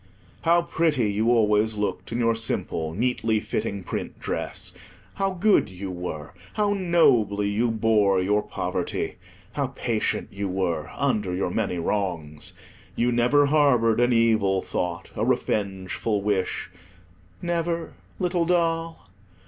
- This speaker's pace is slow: Yes, slow, 125 wpm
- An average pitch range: No, wide, 6.7 semitones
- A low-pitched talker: Yes, low, 110 Hz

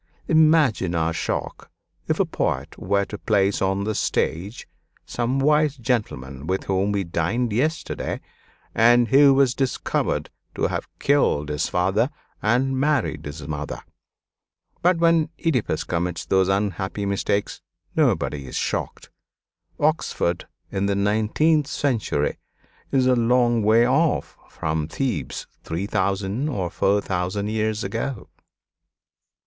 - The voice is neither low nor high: No, low, 105 Hz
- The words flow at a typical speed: No, slow, 125 wpm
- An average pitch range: No, wide, 5.8 semitones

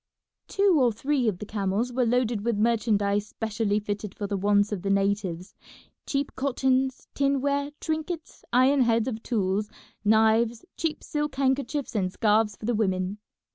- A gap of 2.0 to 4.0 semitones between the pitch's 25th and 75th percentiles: No, average, 4.5 semitones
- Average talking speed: Yes, average, 155 wpm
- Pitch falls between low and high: No, high, 225 Hz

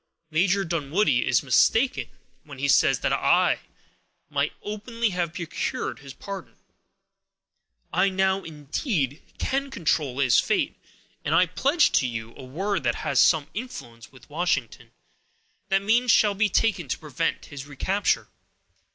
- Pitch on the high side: No, medium, 175 Hz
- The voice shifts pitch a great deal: Yes, wide, 6.9 semitones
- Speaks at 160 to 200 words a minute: No, average, 140 wpm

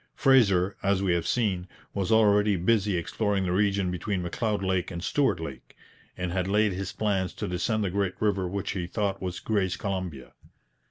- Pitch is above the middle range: No, very low, 95 Hz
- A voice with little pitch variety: Yes, narrow, 2.3 semitones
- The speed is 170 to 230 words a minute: Yes, average, 180 wpm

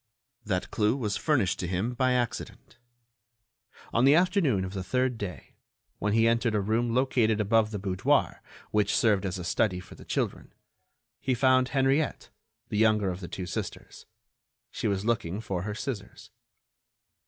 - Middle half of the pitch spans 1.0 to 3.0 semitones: No, average, 4.3 semitones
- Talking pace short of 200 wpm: Yes, average, 165 wpm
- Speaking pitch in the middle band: No, low, 110 Hz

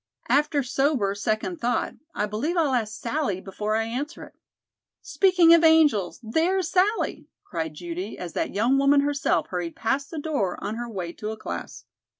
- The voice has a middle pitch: No, high, 245 Hz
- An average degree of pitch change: No, wide, 6.8 semitones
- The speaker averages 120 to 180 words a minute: Yes, average, 175 wpm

